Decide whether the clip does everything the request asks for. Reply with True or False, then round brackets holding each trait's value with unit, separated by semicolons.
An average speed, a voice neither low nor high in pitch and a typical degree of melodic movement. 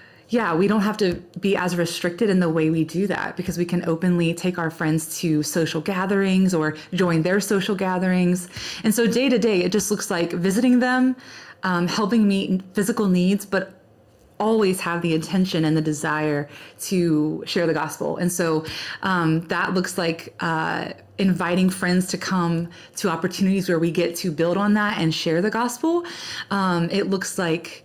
True (185 wpm; 180 Hz; 3.0 semitones)